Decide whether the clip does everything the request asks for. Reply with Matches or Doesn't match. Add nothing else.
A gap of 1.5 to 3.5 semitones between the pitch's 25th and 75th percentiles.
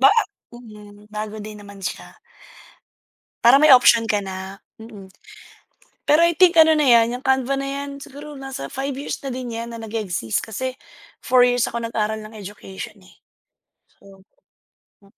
Doesn't match